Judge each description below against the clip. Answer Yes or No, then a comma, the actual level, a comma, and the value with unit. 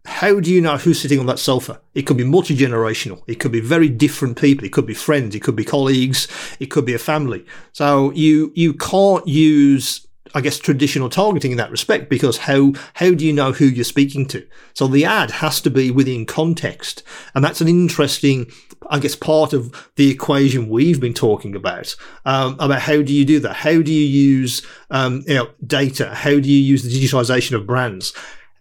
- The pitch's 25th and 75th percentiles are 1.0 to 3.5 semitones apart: Yes, average, 2.8 semitones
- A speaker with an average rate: No, fast, 210 wpm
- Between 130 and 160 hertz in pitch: Yes, medium, 140 Hz